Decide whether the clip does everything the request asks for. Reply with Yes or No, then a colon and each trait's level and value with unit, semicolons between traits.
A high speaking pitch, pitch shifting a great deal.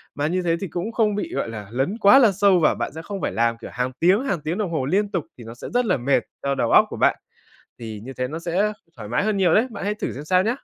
No: medium, 175 Hz; wide, 7.5 semitones